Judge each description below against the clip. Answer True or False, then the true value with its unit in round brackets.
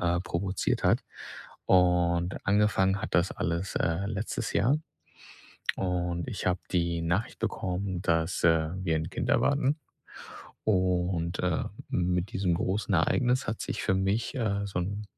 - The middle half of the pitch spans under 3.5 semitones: True (2.6 semitones)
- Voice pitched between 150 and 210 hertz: False (90 Hz)